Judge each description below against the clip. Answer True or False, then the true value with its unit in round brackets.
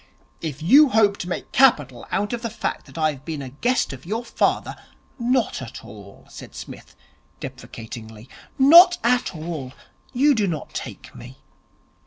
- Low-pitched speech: False (175 Hz)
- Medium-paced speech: True (170 wpm)